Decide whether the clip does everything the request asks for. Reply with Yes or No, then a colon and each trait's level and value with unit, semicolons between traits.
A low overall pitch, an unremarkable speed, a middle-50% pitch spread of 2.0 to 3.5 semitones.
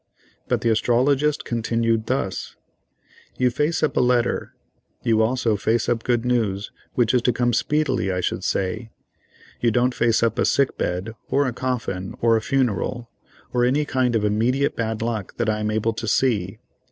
Yes: low, 115 Hz; average, 175 wpm; narrow, 2.4 semitones